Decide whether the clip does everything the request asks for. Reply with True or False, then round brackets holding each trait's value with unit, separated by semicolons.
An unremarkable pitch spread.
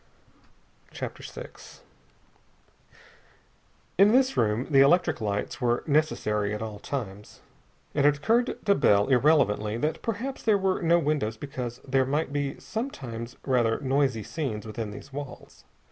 False (5.8 semitones)